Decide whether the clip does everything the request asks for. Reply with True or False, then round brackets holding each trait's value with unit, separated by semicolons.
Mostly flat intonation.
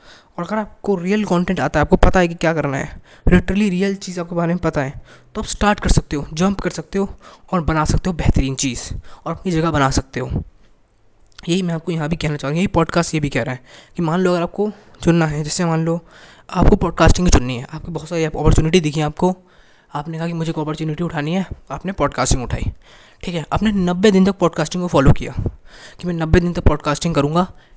False (3.5 semitones)